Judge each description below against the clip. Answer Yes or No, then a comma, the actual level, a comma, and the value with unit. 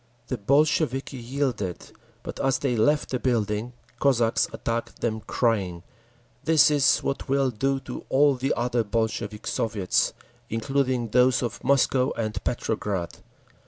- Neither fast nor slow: No, slow, 130 wpm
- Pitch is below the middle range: Yes, low, 125 Hz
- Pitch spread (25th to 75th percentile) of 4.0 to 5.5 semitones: No, average, 3.5 semitones